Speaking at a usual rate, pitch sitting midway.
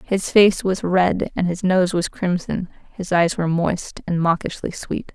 Yes: average, 185 wpm; medium, 180 Hz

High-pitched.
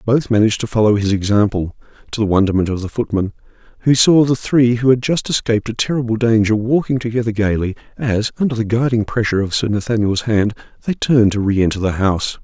No: low, 110 Hz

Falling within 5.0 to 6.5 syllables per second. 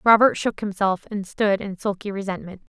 Yes: 5.2 syllables/s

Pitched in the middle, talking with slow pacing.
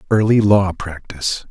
No: very low, 95 Hz; slow, 120 wpm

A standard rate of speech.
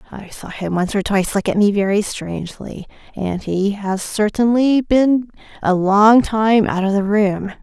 Yes: average, 180 wpm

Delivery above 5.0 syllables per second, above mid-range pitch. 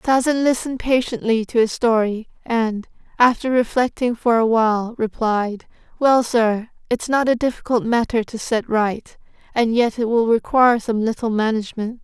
No: 4.8 syllables/s; high, 230 Hz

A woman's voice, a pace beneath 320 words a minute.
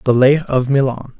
No: male; average, 200 wpm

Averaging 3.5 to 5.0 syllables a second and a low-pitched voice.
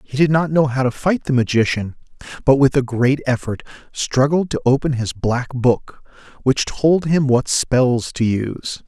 Yes: 4.4 syllables/s; low, 130 Hz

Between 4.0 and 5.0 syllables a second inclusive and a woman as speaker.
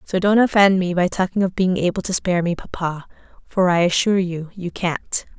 No: 5.4 syllables/s; female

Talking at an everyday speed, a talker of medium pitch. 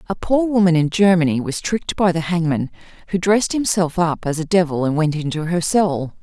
No: fast, 210 wpm; medium, 175 Hz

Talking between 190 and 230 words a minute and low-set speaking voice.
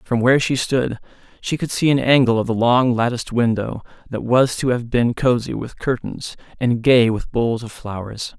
Yes: average, 200 wpm; low, 120 Hz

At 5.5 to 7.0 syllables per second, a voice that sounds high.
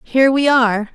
Yes: 6.0 syllables/s; very high, 250 Hz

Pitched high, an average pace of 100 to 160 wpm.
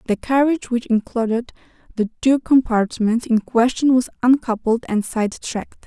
Yes: high, 240 Hz; average, 145 wpm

